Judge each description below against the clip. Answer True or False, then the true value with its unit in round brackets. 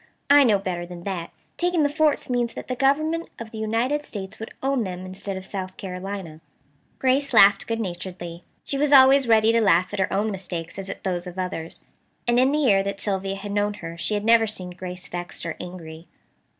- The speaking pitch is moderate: False (200 Hz)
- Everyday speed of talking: False (215 wpm)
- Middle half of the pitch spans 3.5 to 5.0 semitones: True (4.7 semitones)